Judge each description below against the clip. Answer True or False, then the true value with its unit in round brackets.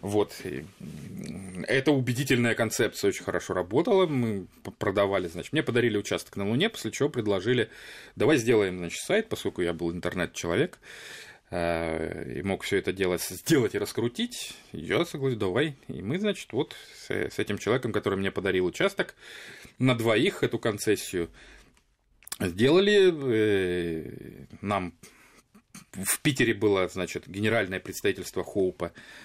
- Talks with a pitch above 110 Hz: False (105 Hz)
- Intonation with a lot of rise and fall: True (7.4 semitones)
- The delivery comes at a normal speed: True (125 wpm)